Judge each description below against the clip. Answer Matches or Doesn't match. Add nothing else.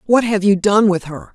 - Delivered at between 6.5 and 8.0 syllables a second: Doesn't match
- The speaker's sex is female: Matches